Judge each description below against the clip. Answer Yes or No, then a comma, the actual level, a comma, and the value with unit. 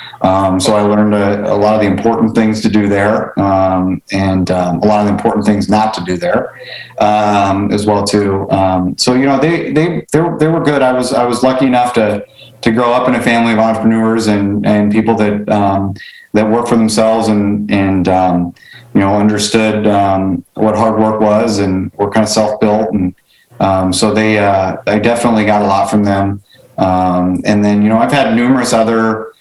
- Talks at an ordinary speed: No, fast, 210 wpm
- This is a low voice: Yes, low, 105 Hz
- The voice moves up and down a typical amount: No, narrow, 2.3 semitones